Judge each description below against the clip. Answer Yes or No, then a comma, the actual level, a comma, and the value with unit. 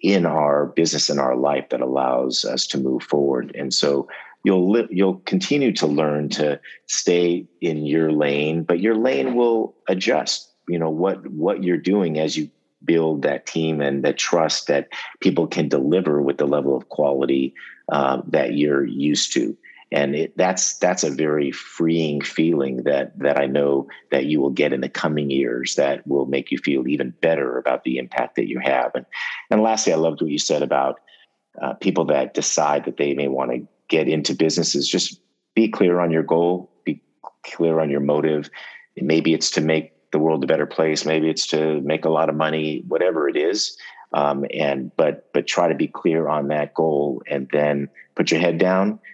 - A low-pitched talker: Yes, very low, 75 Hz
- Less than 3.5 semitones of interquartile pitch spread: Yes, narrow, 2.5 semitones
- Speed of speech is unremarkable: Yes, average, 195 wpm